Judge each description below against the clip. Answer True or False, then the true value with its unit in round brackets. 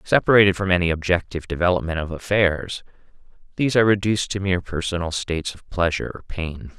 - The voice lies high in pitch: False (90 Hz)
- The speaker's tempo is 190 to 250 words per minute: False (160 wpm)